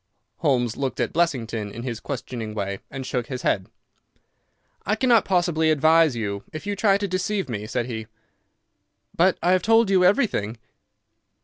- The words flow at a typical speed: Yes, average, 165 wpm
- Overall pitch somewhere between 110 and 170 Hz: Yes, medium, 140 Hz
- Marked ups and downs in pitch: Yes, wide, 8.1 semitones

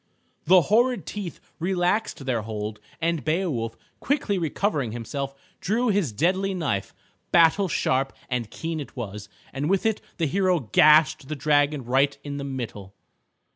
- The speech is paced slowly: No, average, 145 wpm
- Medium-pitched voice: Yes, medium, 150 Hz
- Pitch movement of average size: No, wide, 6.2 semitones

